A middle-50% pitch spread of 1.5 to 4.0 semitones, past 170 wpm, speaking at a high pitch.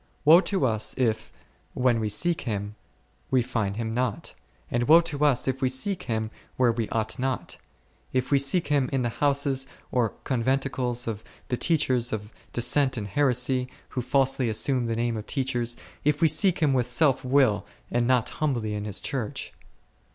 No: average, 3.1 semitones; average, 180 wpm; low, 125 Hz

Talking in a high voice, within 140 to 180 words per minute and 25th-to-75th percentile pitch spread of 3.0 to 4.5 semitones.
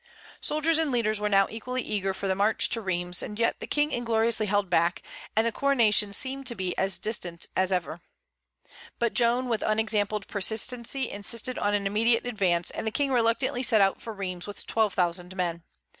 No: high, 215 Hz; average, 190 wpm; average, 3.5 semitones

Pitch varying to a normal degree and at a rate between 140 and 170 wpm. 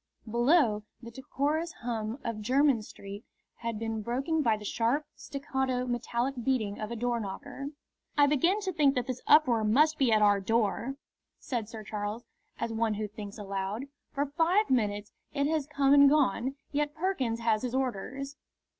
Yes: average, 4.5 semitones; average, 165 wpm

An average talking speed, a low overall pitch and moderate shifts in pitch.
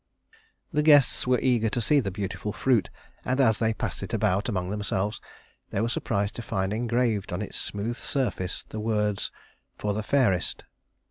Yes: average, 175 wpm; low, 110 Hz; average, 3.1 semitones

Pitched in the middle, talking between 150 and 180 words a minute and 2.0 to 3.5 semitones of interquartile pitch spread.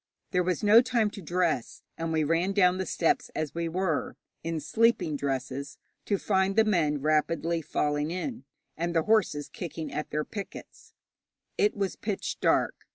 No: medium, 170 Hz; average, 165 wpm; average, 4.3 semitones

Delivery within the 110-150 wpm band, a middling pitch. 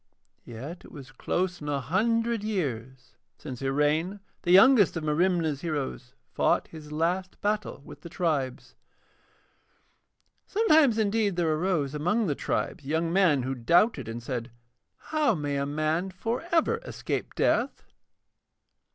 Yes: slow, 135 wpm; medium, 165 Hz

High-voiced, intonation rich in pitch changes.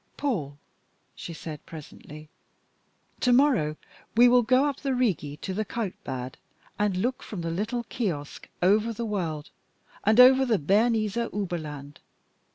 Yes: high, 205 Hz; wide, 7.5 semitones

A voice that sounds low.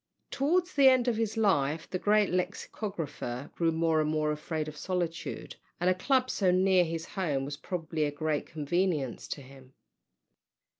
No: medium, 165 Hz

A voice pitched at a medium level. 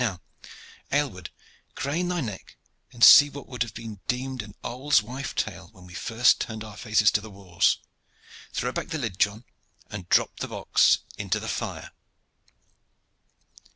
No: low, 115 Hz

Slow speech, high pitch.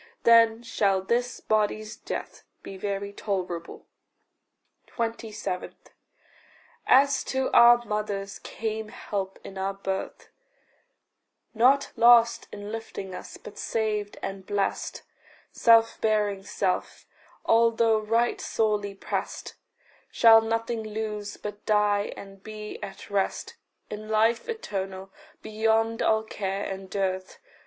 Yes: slow, 110 wpm; high, 215 Hz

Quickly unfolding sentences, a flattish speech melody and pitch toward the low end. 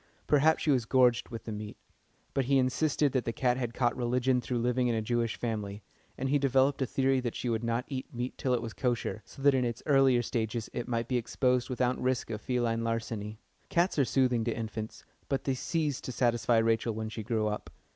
Yes: fast, 225 wpm; narrow, 2.3 semitones; low, 120 Hz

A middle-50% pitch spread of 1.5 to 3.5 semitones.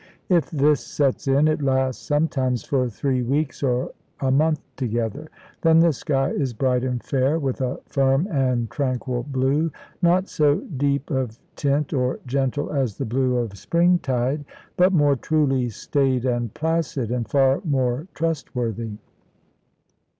Yes: average, 3.0 semitones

